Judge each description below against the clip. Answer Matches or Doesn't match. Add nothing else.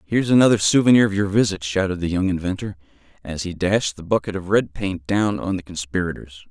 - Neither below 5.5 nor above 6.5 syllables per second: Matches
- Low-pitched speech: Matches